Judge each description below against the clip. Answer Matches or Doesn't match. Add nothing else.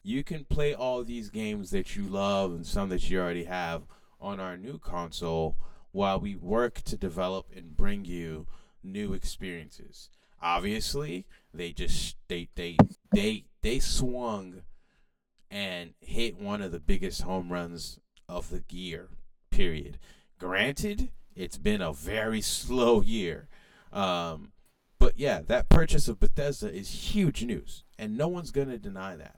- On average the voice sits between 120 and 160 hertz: Doesn't match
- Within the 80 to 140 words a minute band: Doesn't match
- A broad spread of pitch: Matches